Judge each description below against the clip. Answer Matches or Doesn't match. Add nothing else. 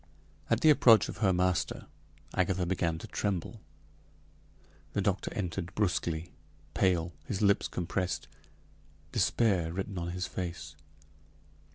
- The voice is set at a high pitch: Doesn't match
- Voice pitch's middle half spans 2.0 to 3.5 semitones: Matches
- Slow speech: Matches